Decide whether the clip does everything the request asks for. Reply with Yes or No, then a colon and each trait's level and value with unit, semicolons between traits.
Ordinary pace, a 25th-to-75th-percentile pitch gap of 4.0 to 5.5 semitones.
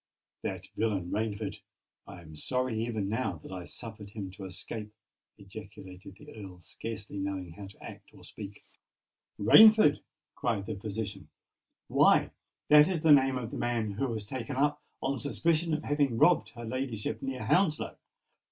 Yes: average, 160 wpm; average, 5.1 semitones